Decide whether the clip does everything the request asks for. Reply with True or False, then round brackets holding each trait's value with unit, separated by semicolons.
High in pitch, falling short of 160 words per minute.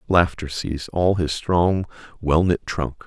False (85 Hz; 135 wpm)